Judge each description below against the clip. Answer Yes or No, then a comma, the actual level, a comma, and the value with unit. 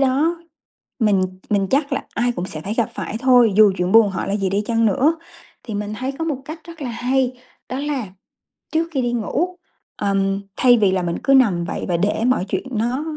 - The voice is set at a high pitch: Yes, high, 235 Hz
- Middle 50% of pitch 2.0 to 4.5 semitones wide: No, average, 5.2 semitones